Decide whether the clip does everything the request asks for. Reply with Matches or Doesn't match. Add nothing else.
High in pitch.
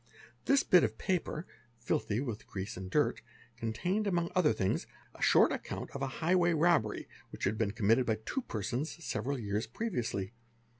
Doesn't match